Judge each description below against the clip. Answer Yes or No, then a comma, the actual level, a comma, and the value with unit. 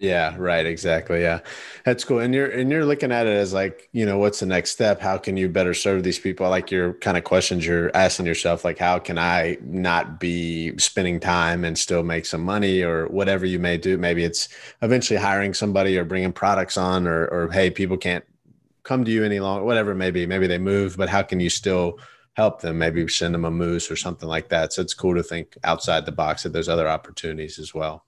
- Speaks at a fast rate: Yes, fast, 235 wpm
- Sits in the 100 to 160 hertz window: No, very low, 90 Hz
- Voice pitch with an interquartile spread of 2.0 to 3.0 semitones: Yes, narrow, 2.4 semitones